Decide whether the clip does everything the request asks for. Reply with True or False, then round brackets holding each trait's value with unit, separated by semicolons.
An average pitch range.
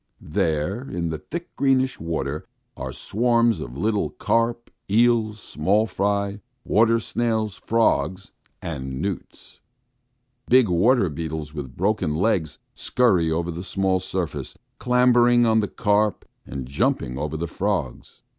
False (6.2 semitones)